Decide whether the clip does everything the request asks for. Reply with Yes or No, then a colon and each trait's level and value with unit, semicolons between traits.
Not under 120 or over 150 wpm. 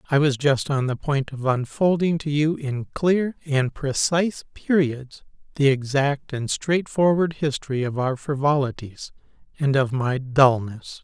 Yes: average, 145 wpm